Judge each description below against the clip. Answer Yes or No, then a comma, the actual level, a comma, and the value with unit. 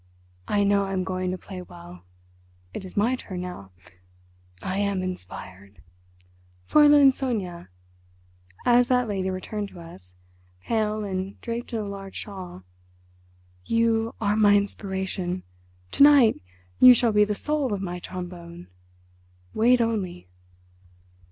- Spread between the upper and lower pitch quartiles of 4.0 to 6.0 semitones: Yes, average, 4.3 semitones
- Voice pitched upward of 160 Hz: Yes, high, 190 Hz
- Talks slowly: Yes, slow, 125 wpm